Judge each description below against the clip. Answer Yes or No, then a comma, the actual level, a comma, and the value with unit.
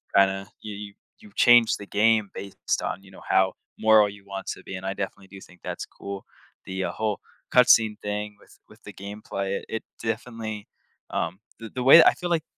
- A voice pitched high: No, low, 105 Hz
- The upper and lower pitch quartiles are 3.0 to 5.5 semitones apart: No, narrow, 2.4 semitones